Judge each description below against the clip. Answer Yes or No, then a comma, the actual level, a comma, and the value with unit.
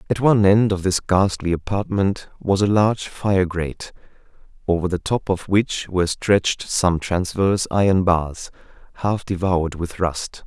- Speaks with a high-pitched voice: No, very low, 95 Hz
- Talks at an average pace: Yes, average, 155 wpm